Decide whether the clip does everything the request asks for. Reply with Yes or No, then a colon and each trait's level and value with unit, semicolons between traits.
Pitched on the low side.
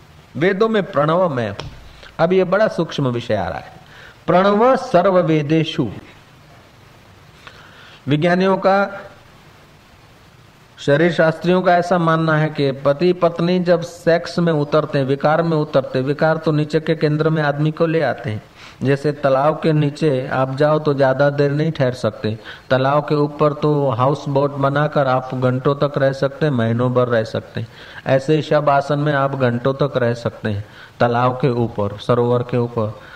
No: medium, 145 Hz